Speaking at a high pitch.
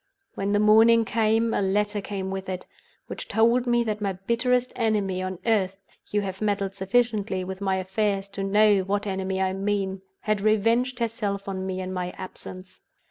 Yes: high, 200 Hz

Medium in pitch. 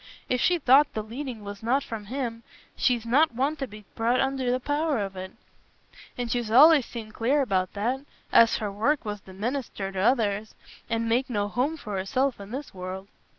No: high, 235 Hz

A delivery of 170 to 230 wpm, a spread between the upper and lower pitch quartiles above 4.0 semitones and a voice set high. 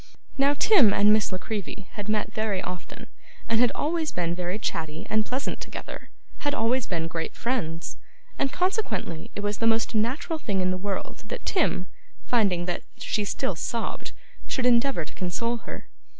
Yes: average, 175 wpm; average, 5.3 semitones; high, 215 Hz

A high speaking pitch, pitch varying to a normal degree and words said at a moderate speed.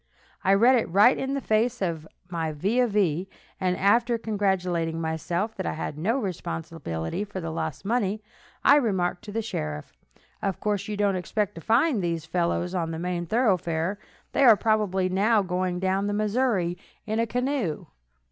Yes: high, 195 Hz; average, 4.2 semitones; average, 175 wpm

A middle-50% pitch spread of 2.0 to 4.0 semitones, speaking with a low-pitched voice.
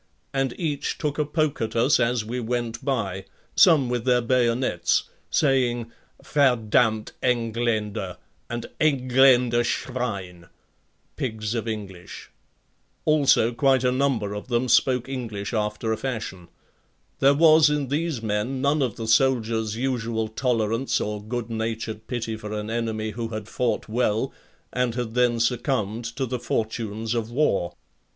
Yes: average, 2.9 semitones; low, 120 Hz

